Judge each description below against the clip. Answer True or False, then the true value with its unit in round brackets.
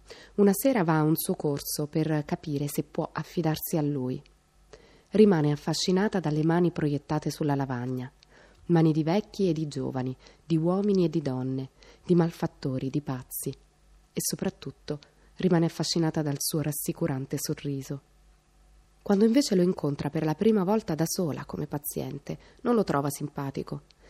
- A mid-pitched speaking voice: True (155 Hz)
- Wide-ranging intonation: False (3.4 semitones)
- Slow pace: False (150 wpm)